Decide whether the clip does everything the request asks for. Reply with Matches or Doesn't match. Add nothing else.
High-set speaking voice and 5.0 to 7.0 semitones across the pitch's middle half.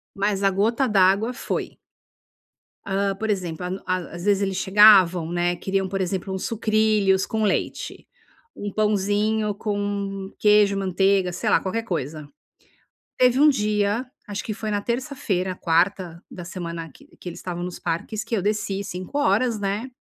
Doesn't match